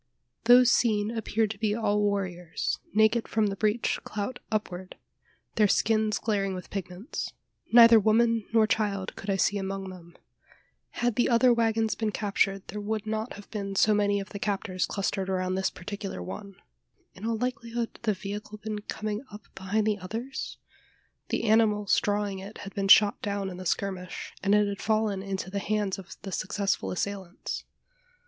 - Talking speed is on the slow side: No, average, 175 wpm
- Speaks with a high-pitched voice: Yes, high, 205 Hz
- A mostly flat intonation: Yes, narrow, 2.0 semitones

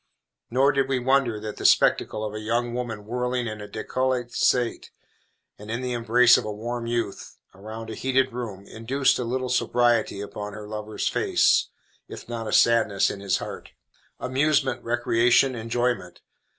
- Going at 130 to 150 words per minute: No, average, 165 wpm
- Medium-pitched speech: No, low, 120 Hz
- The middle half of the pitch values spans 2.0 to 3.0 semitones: Yes, narrow, 2.5 semitones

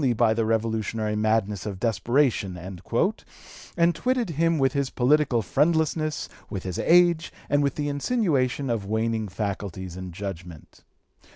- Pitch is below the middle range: Yes, low, 115 Hz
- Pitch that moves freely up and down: Yes, wide, 6.6 semitones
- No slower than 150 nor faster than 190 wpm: No, slow, 135 wpm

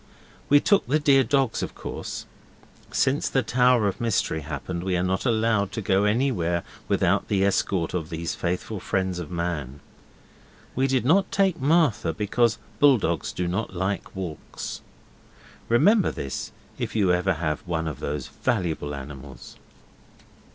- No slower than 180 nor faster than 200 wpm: No, average, 150 wpm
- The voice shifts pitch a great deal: Yes, wide, 6.5 semitones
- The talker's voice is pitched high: No, very low, 95 Hz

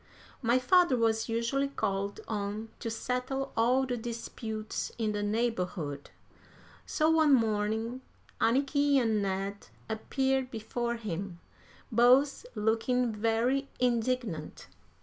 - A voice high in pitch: Yes, high, 230 Hz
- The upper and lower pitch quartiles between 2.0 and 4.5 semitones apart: Yes, average, 3.1 semitones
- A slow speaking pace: Yes, slow, 110 wpm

